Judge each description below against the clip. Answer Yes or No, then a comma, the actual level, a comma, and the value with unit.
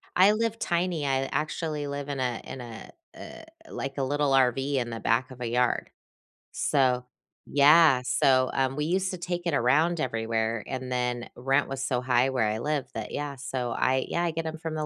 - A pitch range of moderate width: Yes, average, 3.6 semitones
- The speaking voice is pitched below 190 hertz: Yes, low, 135 Hz